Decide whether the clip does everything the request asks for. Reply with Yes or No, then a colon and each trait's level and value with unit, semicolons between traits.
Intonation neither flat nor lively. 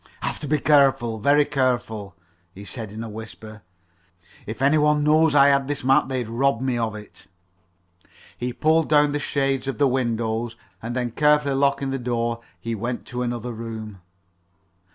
Yes: average, 3.7 semitones